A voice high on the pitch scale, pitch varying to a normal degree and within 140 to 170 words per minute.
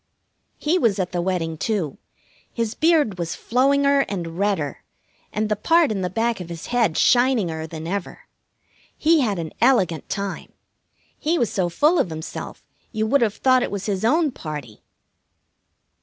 No: high, 205 Hz; wide, 6.9 semitones; average, 165 wpm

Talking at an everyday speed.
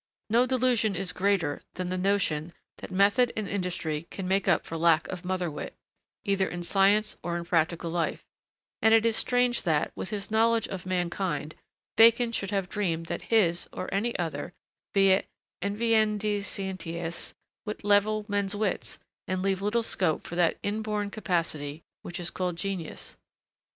Yes: average, 160 wpm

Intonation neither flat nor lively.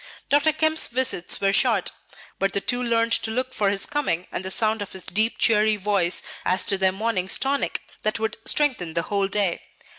Yes: average, 4.2 semitones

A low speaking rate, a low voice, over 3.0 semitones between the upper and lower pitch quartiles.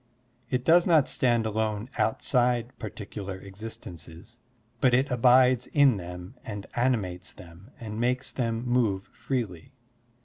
Yes: slow, 125 wpm; low, 115 Hz; average, 4.1 semitones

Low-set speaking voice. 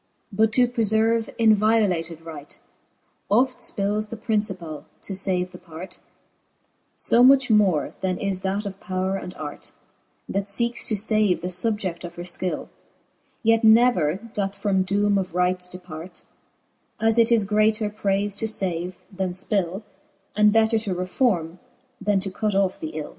No: high, 200 Hz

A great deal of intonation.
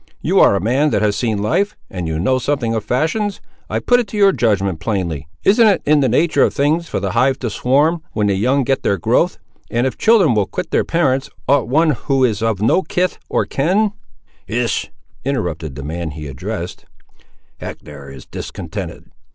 Yes: wide, 7.8 semitones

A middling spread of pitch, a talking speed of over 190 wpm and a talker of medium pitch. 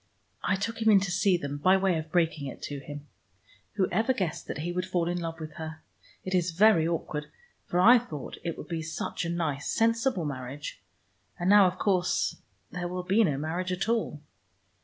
Yes: average, 3.5 semitones; average, 200 wpm; medium, 175 Hz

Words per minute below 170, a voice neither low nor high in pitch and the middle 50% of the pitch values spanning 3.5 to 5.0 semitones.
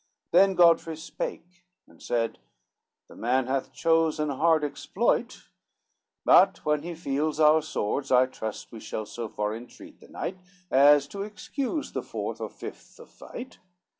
Yes: average, 155 wpm; medium, 150 Hz; average, 4.6 semitones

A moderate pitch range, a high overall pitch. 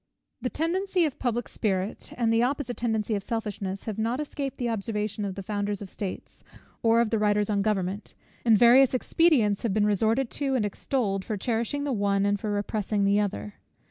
Yes: average, 3.2 semitones; high, 220 Hz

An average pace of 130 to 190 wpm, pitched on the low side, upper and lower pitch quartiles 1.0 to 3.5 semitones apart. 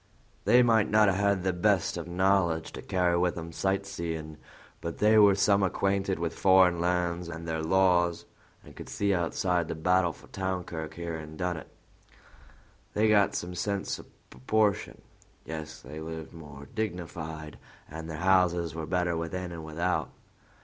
Yes: average, 165 wpm; very low, 90 Hz; average, 2.8 semitones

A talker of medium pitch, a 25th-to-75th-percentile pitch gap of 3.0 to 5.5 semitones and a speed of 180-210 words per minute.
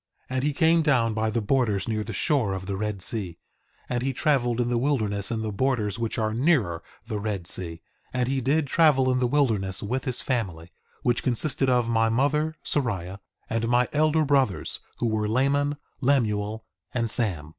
No: low, 120 Hz; average, 4.2 semitones; average, 190 wpm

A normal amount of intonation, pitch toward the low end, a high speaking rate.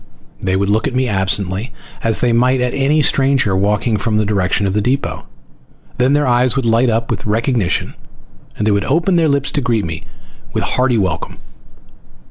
No: average, 4.3 semitones; low, 115 Hz; average, 190 wpm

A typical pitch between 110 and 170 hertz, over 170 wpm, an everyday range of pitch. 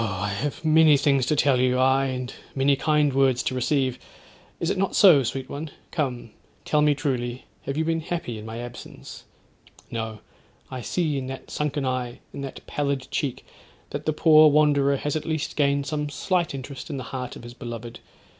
Yes: medium, 140 Hz; average, 190 wpm; average, 3.0 semitones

